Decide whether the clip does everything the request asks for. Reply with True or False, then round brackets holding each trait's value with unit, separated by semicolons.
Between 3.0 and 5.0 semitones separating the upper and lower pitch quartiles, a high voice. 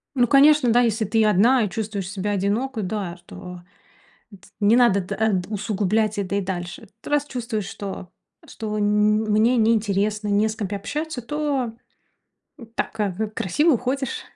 True (3.3 semitones; 215 Hz)